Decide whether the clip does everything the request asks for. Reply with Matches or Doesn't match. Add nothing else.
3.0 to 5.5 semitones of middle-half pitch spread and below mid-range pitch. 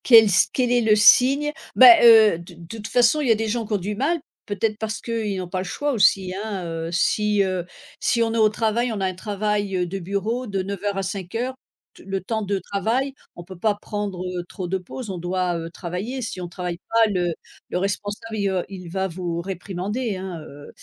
Doesn't match